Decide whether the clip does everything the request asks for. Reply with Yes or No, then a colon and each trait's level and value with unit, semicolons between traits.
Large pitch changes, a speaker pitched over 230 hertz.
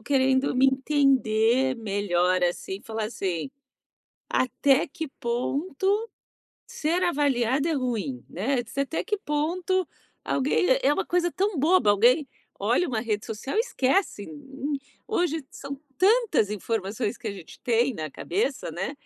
Yes: wide, 6.8 semitones; very high, 265 Hz